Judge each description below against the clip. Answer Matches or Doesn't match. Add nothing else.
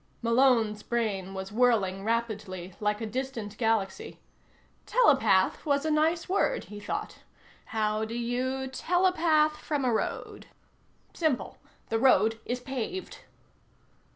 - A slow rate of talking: Matches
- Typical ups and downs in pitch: Matches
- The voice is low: Doesn't match